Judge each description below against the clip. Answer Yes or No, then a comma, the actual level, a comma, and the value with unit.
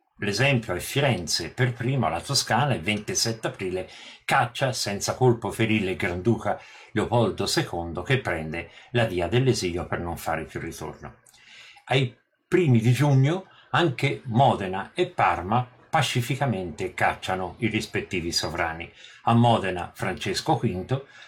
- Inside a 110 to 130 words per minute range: Yes, average, 125 wpm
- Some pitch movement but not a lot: No, wide, 6.1 semitones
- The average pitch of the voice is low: Yes, low, 115 Hz